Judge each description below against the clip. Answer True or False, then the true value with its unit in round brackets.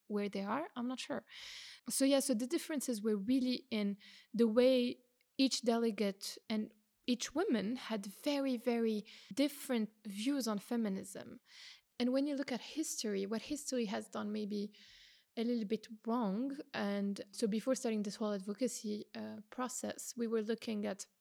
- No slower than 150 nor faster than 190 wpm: True (160 wpm)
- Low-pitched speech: False (230 Hz)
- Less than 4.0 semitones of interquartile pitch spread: True (3.4 semitones)